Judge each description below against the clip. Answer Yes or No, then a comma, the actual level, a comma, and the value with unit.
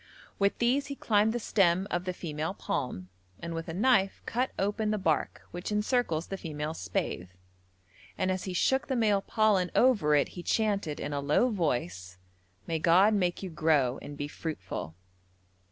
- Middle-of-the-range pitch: Yes, medium, 180 Hz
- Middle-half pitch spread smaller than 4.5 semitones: No, wide, 5.6 semitones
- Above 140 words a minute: Yes, average, 175 wpm